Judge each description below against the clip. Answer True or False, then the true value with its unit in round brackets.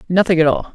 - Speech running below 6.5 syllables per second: False (7.1 syllables/s)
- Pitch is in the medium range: True (170 Hz)